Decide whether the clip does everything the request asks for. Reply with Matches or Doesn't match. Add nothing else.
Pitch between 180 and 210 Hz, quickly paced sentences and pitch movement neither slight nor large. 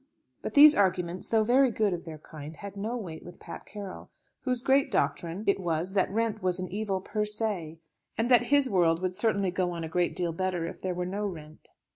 Matches